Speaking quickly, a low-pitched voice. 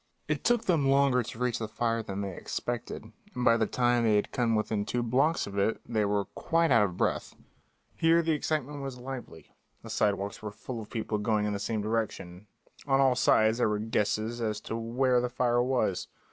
Yes: fast, 210 wpm; low, 115 Hz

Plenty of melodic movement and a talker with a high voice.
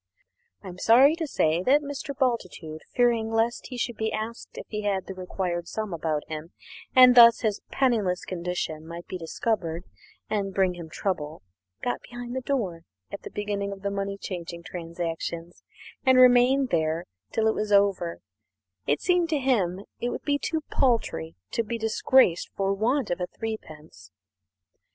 Yes: wide, 5.9 semitones; high, 200 Hz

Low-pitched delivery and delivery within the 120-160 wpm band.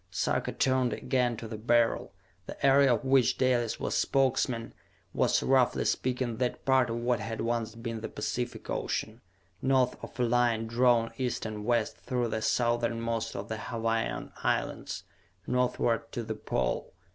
Yes: low, 120 Hz; average, 155 wpm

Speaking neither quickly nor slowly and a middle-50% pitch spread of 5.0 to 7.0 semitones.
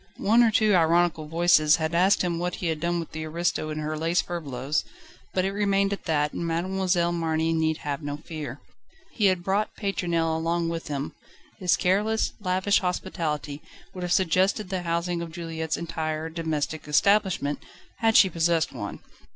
No: average, 175 wpm; average, 2.7 semitones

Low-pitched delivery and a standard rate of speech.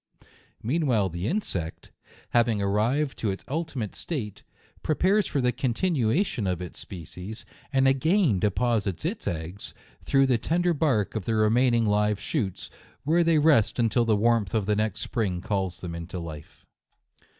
Yes: low, 110 Hz; average, 155 wpm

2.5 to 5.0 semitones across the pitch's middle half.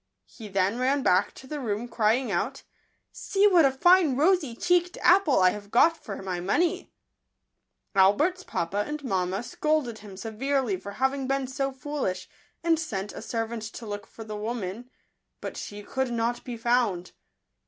No: wide, 5.6 semitones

